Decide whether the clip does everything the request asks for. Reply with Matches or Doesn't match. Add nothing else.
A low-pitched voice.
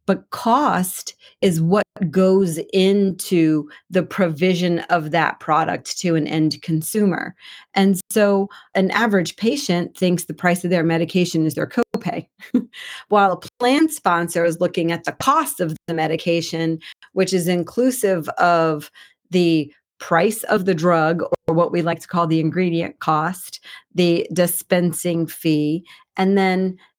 Doesn't match